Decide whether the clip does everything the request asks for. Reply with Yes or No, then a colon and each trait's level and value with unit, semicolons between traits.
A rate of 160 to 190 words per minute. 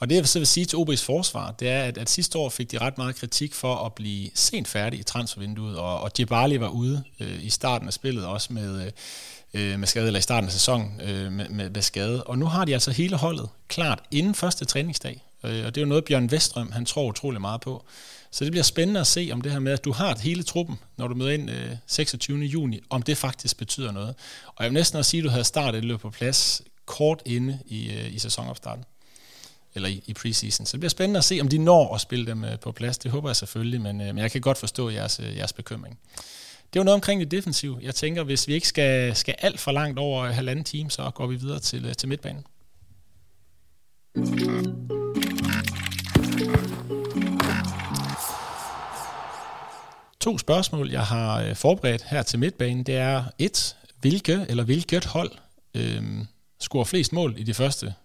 No: average, 205 wpm